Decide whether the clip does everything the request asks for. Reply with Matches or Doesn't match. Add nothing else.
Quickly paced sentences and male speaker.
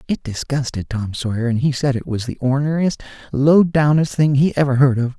Matches